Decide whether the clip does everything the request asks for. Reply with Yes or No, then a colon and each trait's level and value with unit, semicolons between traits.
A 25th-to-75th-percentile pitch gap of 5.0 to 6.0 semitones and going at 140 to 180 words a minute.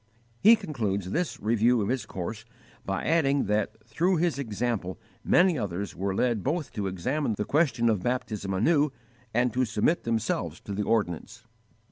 Yes: wide, 5.6 semitones; average, 160 wpm